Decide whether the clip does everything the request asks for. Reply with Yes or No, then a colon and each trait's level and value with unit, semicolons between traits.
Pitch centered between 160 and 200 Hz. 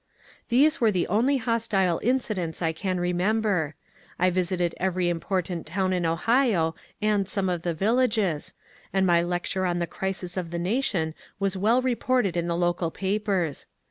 Yes: medium, 185 Hz